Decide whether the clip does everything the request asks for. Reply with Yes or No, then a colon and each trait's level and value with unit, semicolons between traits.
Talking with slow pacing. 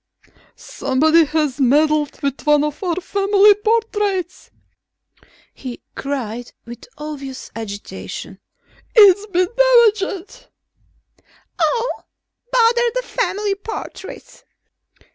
Yes: slow, 85 wpm